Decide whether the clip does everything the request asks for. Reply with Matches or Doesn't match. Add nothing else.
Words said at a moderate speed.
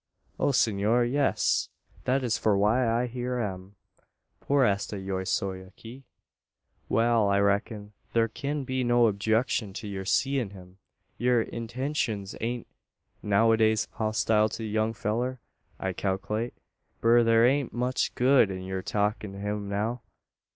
Matches